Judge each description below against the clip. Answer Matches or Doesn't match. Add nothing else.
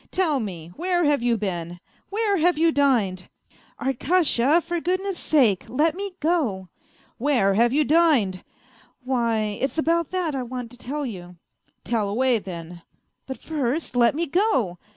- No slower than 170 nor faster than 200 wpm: Matches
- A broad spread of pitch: Matches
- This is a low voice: Doesn't match